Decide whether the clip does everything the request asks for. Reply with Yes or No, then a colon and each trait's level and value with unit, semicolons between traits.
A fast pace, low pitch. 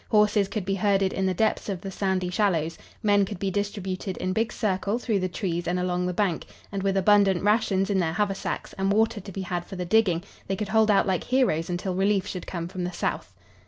No: fast, 235 wpm; high, 195 Hz